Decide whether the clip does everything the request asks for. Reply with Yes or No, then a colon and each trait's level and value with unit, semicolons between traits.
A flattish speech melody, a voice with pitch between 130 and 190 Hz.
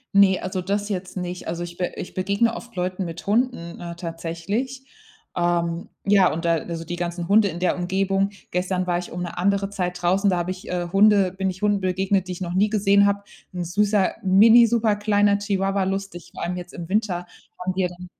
Yes: narrow, 2.3 semitones; medium, 185 Hz